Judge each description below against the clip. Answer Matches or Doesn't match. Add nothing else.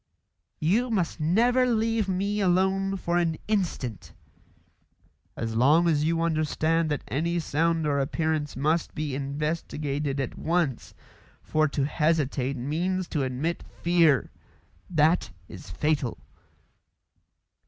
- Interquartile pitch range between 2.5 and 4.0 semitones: Matches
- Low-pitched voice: Doesn't match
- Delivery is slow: Matches